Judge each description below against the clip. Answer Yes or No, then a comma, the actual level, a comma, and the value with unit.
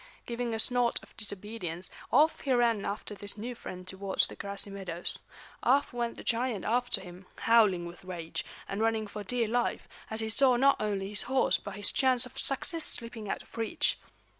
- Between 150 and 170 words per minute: No, average, 190 wpm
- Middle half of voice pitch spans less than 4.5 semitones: Yes, average, 3.5 semitones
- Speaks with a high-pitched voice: Yes, high, 220 Hz